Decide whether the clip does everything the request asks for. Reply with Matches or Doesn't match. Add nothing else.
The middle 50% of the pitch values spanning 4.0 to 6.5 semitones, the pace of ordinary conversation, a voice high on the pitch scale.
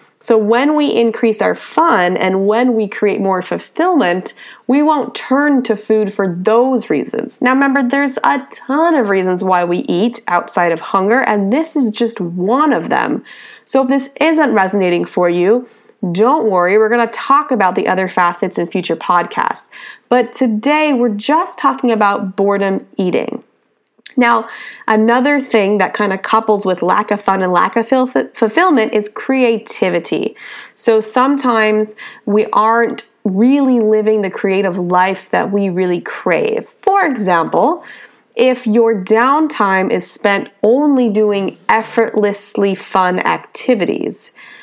Matches